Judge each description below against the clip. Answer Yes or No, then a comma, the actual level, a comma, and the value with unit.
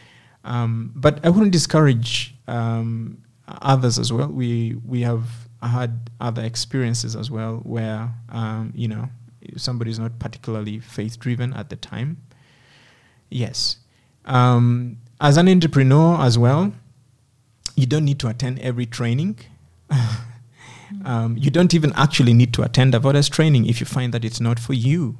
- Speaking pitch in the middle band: No, low, 120 Hz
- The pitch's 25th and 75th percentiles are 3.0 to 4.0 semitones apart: No, narrow, 2.5 semitones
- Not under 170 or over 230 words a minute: No, average, 150 wpm